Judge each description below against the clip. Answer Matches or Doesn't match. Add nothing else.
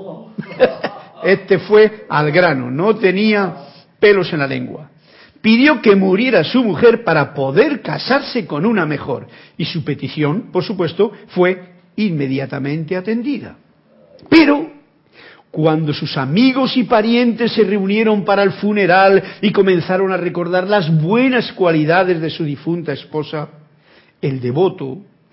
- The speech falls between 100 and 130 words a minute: Matches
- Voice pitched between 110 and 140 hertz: Doesn't match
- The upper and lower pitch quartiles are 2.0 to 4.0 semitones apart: Doesn't match